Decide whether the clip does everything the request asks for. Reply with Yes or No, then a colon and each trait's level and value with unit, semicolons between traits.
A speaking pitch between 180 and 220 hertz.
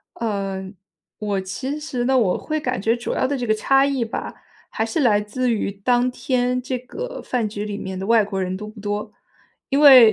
No: high, 230 Hz